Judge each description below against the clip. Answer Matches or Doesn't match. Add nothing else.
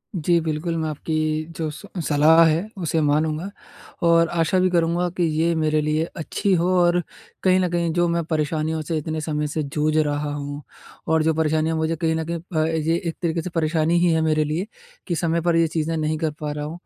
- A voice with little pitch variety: Matches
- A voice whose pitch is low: Doesn't match